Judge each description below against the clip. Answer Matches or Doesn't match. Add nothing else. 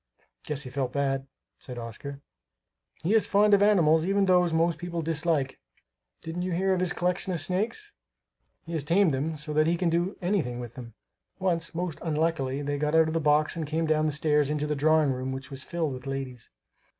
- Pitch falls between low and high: Matches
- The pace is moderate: Doesn't match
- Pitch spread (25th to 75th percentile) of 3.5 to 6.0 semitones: Matches